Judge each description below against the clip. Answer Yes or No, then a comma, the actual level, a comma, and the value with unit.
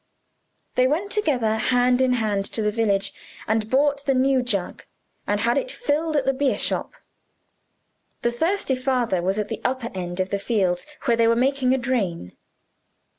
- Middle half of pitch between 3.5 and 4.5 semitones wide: Yes, average, 4.2 semitones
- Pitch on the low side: No, high, 245 Hz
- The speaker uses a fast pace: No, average, 175 wpm